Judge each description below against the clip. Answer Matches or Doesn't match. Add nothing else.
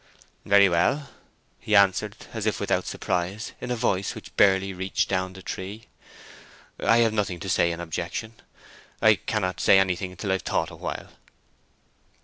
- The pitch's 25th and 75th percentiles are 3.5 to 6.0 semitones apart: Doesn't match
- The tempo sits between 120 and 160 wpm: Matches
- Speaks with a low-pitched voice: Matches